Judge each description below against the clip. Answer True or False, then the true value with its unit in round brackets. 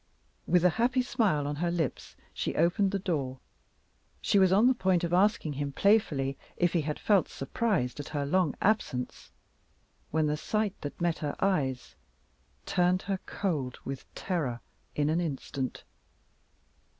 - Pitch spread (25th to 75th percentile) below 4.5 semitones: False (5.2 semitones)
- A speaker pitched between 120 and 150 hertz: False (170 Hz)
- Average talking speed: True (155 wpm)